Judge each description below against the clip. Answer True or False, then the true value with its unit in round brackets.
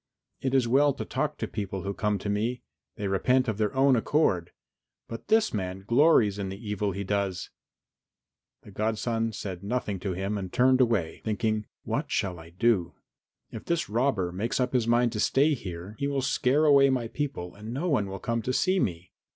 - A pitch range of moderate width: True (4.7 semitones)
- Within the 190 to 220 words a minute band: True (200 wpm)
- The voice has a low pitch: True (110 Hz)